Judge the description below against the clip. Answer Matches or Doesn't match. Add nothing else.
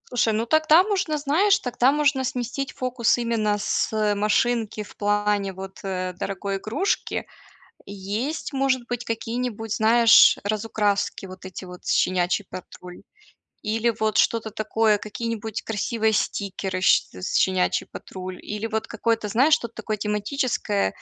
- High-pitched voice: Matches